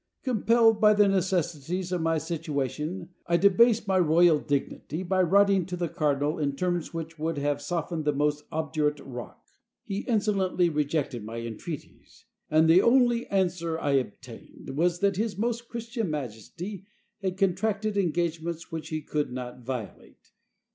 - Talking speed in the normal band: Yes, average, 150 wpm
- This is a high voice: No, medium, 170 Hz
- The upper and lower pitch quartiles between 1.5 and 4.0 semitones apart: No, average, 4.6 semitones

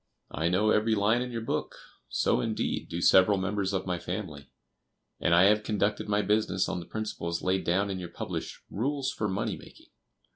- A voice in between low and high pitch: No, low, 100 Hz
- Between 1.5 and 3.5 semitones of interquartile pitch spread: Yes, average, 2.9 semitones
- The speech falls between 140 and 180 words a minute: No, average, 190 wpm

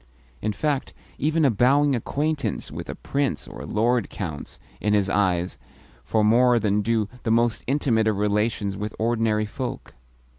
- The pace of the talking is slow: No, average, 160 wpm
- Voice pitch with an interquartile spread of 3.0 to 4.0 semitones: Yes, average, 3.3 semitones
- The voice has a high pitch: No, low, 110 Hz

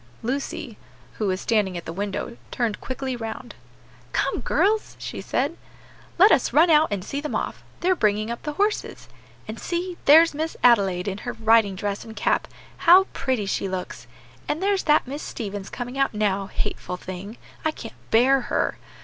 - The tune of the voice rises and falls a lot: Yes, wide, 6.7 semitones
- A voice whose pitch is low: No, high, 235 Hz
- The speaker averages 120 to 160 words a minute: No, average, 175 wpm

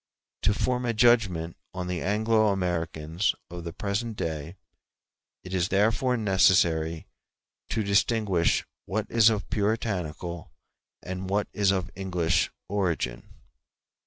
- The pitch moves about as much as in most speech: Yes, average, 3.9 semitones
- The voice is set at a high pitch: No, very low, 95 Hz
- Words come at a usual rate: No, slow, 120 wpm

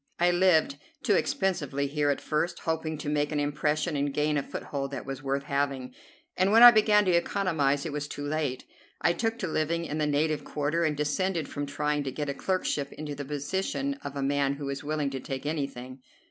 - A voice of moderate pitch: Yes, medium, 150 Hz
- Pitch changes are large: No, average, 3.0 semitones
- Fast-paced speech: Yes, fast, 215 wpm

